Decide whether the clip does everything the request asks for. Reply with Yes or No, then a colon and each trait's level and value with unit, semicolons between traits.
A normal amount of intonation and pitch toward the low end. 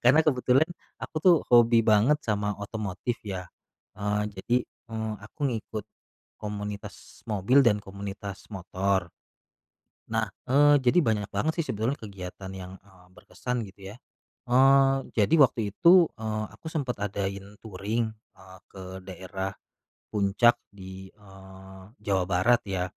Yes: average, 3.9 semitones; low, 105 Hz